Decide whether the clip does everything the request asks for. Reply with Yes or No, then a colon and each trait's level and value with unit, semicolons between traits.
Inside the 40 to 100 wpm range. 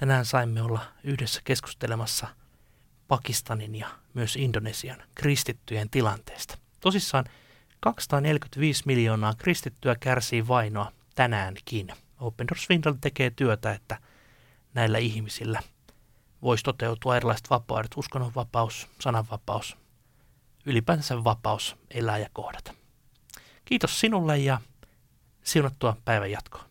Yes: slow, 95 wpm